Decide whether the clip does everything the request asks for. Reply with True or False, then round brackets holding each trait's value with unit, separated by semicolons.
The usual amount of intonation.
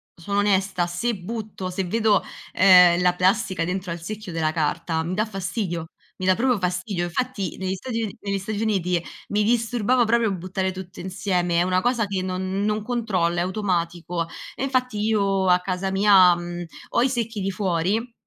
True (3.2 semitones)